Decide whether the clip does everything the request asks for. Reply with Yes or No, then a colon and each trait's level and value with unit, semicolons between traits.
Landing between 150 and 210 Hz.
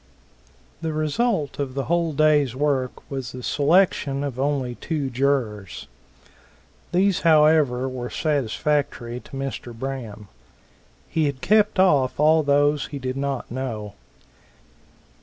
No: medium, 140 Hz